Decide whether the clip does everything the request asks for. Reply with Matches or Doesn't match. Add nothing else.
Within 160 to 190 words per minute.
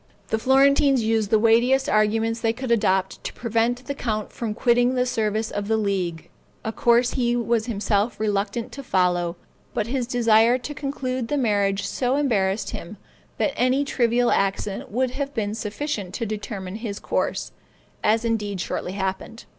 Matches